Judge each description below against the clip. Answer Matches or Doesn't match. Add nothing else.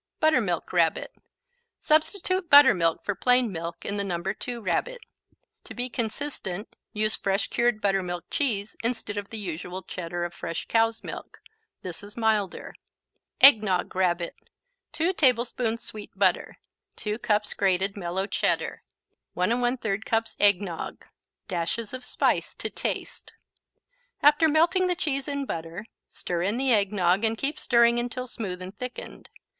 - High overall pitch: Matches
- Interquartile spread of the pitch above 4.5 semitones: Matches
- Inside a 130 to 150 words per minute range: Matches